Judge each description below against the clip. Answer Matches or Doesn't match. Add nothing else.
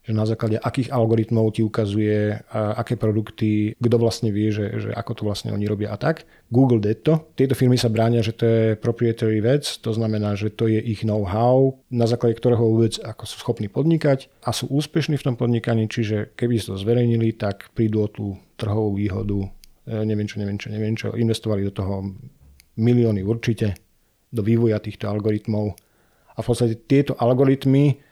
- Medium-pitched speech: Doesn't match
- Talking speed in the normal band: Doesn't match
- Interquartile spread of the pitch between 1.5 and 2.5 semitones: Matches